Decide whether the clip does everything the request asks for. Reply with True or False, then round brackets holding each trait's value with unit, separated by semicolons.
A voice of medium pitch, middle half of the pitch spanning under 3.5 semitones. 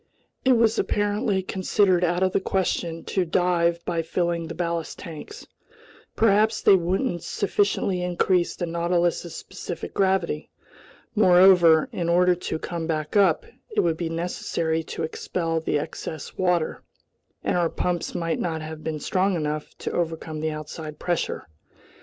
True (175 Hz; 2.4 semitones)